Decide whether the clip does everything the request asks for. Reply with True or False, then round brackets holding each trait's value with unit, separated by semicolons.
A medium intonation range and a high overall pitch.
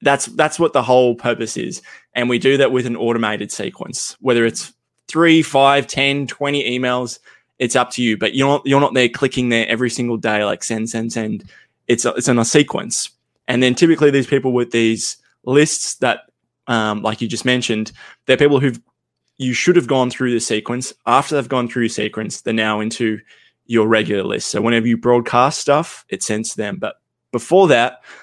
False (3.2 semitones; 125 Hz)